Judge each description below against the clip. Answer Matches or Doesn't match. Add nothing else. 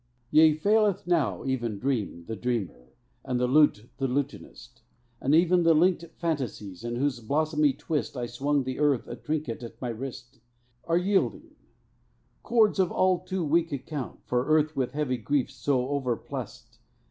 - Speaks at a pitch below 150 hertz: Matches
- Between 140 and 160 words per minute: Matches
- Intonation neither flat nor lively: Matches